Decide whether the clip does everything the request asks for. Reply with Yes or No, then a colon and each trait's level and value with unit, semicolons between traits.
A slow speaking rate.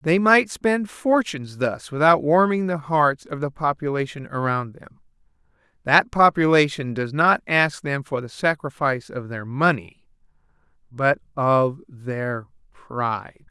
Yes: slow, 130 wpm